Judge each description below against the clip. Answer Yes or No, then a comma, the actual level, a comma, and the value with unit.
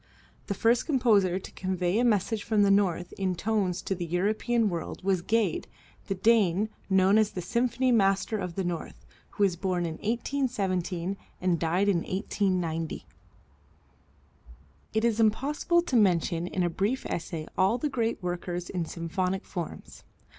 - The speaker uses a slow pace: No, average, 155 wpm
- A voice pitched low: No, high, 195 Hz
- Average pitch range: Yes, average, 3.8 semitones